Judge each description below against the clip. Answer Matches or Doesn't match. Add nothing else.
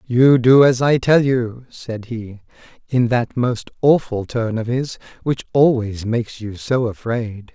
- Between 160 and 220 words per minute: Matches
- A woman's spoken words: Doesn't match